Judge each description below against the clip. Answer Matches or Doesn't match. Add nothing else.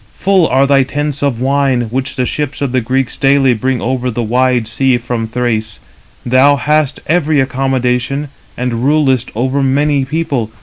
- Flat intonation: Matches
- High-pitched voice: Doesn't match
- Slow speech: Doesn't match